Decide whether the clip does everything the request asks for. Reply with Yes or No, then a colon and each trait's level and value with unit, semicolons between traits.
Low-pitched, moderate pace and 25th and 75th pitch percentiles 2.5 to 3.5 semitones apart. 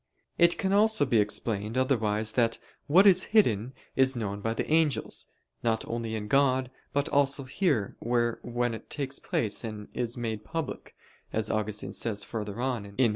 No: low, 120 Hz; average, 180 wpm; average, 4.1 semitones